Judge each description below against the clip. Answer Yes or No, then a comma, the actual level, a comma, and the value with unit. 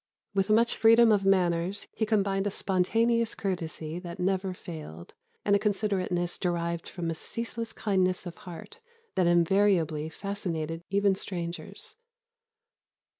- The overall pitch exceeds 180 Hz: Yes, high, 190 Hz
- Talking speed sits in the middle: No, slow, 125 wpm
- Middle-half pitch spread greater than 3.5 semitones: No, average, 3.1 semitones